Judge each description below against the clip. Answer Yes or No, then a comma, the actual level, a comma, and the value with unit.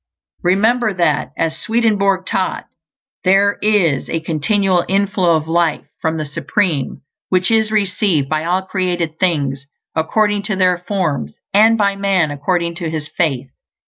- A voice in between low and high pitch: Yes, medium, 180 Hz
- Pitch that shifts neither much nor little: Yes, average, 3.9 semitones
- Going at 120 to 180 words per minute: Yes, average, 145 wpm